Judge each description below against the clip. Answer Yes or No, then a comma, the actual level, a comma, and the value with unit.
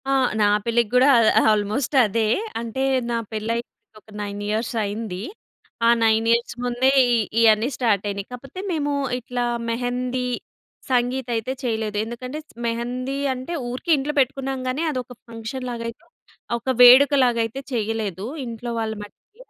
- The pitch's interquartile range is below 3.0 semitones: Yes, narrow, 2.5 semitones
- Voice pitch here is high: Yes, high, 240 Hz